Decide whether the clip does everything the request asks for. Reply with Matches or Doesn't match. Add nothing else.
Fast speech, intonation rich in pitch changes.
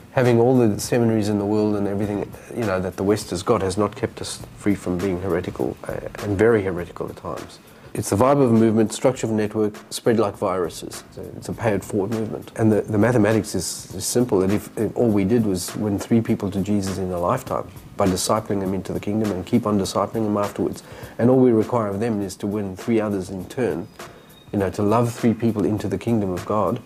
Doesn't match